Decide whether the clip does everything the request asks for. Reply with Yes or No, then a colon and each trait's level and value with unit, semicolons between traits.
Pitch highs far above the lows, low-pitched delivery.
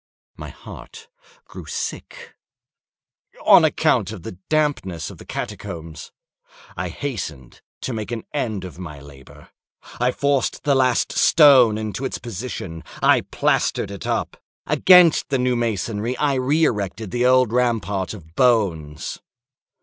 Yes: wide, 6.3 semitones; low, 115 Hz